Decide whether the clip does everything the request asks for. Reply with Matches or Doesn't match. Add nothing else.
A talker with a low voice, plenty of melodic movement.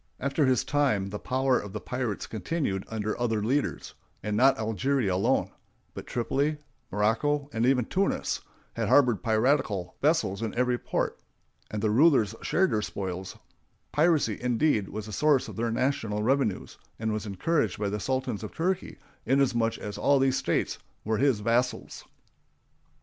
Doesn't match